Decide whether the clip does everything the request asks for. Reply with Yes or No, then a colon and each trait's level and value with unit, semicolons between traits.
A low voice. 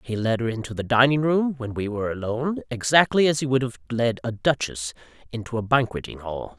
Yes: low, 120 Hz